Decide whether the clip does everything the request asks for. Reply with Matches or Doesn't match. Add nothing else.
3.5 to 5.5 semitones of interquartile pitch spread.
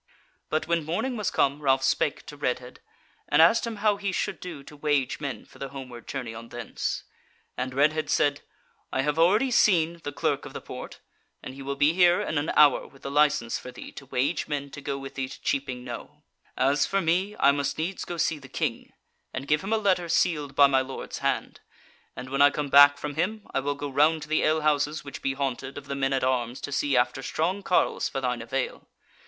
Doesn't match